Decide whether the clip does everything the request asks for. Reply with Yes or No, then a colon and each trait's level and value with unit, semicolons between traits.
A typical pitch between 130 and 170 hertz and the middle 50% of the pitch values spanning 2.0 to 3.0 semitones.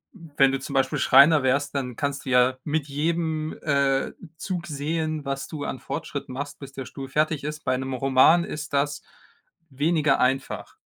Yes: medium, 140 Hz; narrow, 2.4 semitones